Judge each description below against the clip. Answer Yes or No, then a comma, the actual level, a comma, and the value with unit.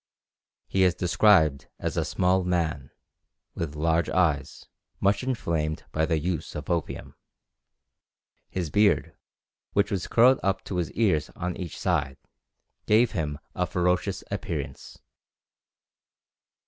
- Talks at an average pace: No, slow, 120 wpm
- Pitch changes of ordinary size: Yes, average, 3.8 semitones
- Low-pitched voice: Yes, very low, 85 Hz